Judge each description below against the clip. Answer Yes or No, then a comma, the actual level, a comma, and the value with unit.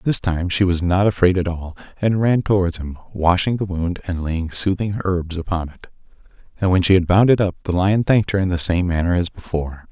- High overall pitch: No, very low, 90 Hz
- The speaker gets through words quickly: Yes, fast, 230 wpm